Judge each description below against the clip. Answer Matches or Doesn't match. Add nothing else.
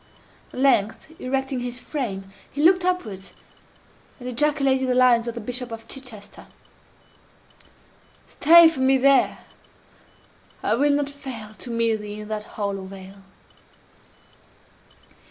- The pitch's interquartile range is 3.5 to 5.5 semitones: Matches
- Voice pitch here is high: Matches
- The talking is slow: Matches